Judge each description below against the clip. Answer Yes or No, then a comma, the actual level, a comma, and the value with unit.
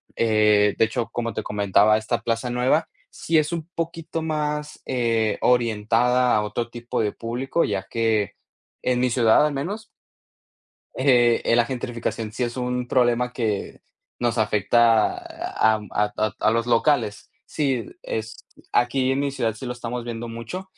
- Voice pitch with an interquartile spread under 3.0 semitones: Yes, narrow, 2.6 semitones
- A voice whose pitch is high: No, low, 120 Hz